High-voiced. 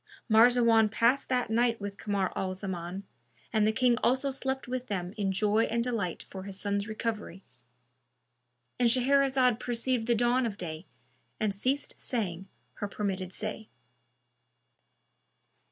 Yes: high, 215 Hz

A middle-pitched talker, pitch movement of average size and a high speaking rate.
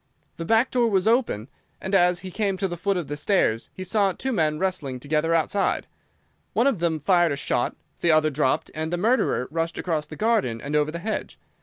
Yes: medium, 175 Hz; average, 4.6 semitones; fast, 220 wpm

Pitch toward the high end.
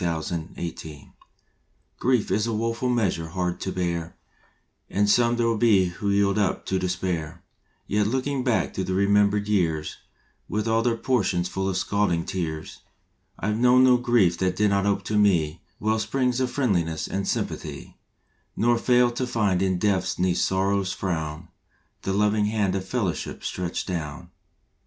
No: low, 100 Hz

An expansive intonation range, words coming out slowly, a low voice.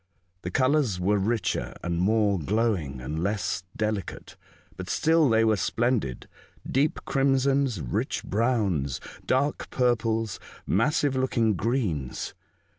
Yes: wide, 5.8 semitones; slow, 115 wpm; low, 110 Hz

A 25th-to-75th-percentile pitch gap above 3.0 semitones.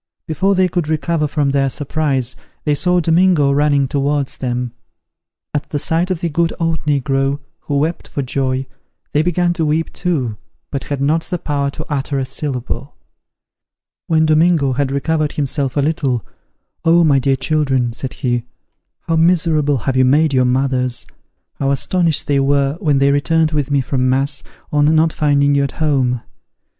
No: average, 2.7 semitones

